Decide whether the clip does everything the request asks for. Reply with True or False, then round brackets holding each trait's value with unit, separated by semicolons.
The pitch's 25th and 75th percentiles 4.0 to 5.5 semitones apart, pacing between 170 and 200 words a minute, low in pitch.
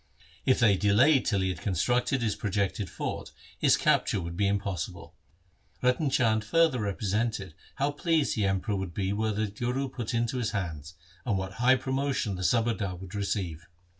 True (4.4 semitones; 175 wpm; 105 Hz)